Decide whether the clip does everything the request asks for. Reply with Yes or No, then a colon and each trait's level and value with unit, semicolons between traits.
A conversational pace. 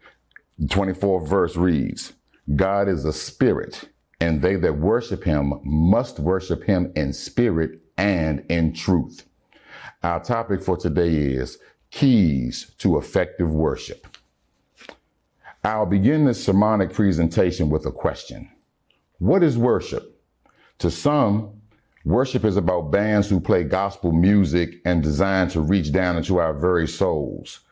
No: slow, 130 wpm